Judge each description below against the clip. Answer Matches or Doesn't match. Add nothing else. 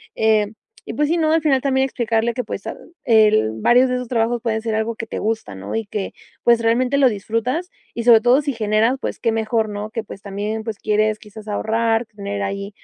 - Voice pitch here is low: Doesn't match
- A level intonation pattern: Matches